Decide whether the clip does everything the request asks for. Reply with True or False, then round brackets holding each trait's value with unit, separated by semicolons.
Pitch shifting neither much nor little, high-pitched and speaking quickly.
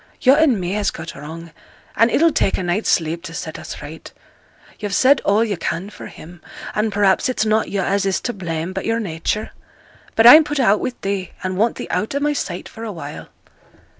True (4.7 semitones; 200 Hz; 215 wpm)